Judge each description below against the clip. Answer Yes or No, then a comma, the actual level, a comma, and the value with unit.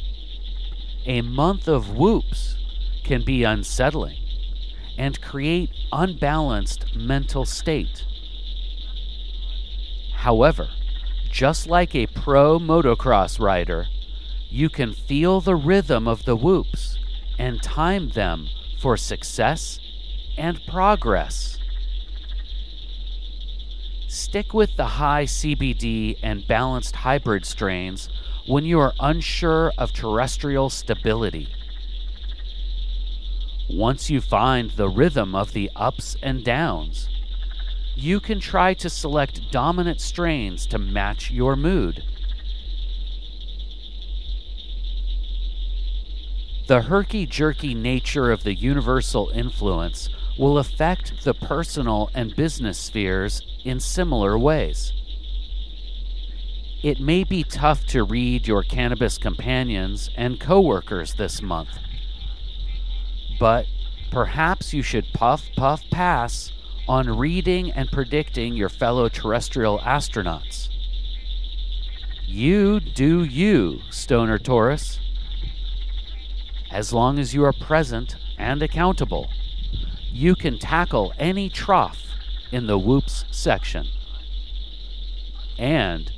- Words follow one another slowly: Yes, slow, 95 wpm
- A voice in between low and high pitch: No, low, 105 Hz